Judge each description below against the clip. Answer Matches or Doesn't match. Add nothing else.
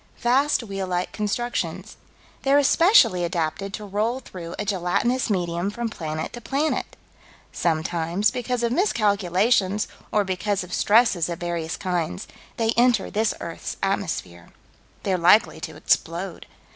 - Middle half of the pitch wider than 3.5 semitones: Matches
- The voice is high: Matches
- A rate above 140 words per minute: Doesn't match